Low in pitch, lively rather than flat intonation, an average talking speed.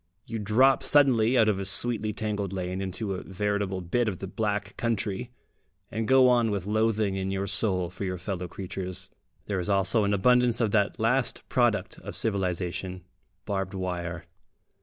No: low, 100 Hz; average, 3.1 semitones; average, 170 wpm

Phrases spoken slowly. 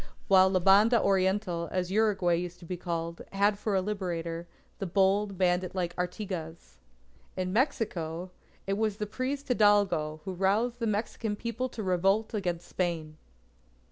No: average, 150 wpm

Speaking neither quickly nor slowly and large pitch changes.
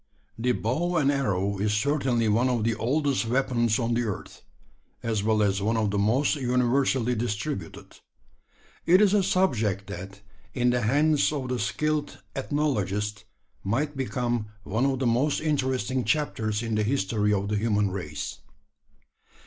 No: average, 155 wpm; average, 4.4 semitones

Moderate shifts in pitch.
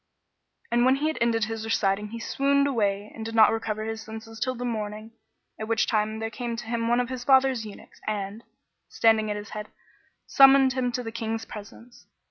No: narrow, 2.3 semitones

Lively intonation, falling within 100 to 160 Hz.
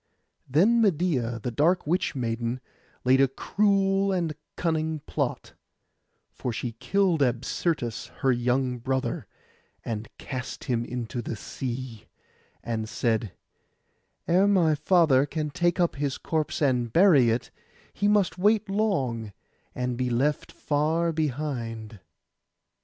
Yes: wide, 6.2 semitones; medium, 140 Hz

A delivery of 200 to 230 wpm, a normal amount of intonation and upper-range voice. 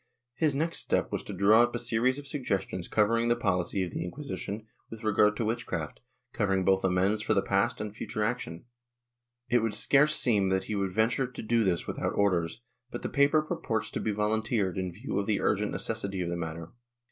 No: fast, 205 wpm; average, 3.8 semitones; low, 105 Hz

